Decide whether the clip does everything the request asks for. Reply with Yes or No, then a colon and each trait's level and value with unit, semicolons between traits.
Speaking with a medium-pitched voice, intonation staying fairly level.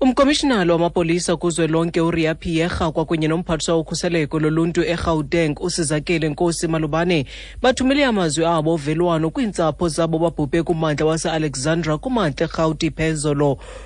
Yes: medium, 165 Hz; narrow, 1.5 semitones